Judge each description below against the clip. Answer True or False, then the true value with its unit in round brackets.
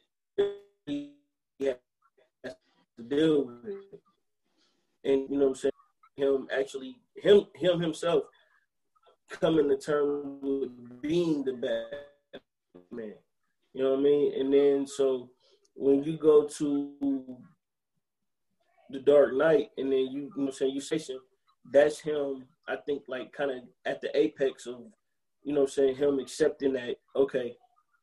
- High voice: False (140 Hz)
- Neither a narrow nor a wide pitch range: True (3.3 semitones)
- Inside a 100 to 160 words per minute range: True (145 wpm)